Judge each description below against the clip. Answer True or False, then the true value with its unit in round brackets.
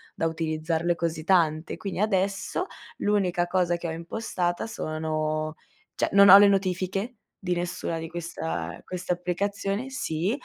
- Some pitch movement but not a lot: True (3.3 semitones)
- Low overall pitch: False (175 Hz)